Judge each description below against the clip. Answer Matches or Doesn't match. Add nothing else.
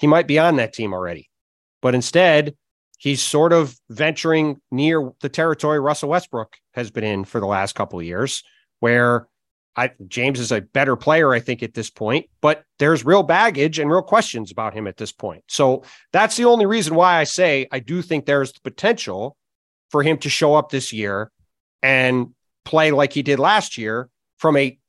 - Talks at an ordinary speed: Matches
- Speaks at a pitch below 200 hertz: Matches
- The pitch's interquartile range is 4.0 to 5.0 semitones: Doesn't match